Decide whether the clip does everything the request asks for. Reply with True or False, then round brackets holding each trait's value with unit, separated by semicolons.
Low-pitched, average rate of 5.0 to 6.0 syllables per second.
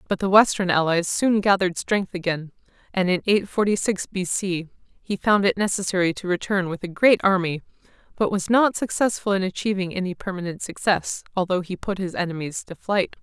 False (190 Hz; 5.4 syllables/s)